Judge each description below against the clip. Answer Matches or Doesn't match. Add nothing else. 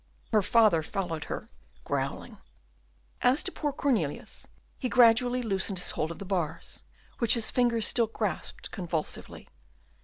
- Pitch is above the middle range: Matches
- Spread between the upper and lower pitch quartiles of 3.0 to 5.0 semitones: Doesn't match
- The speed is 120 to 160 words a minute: Matches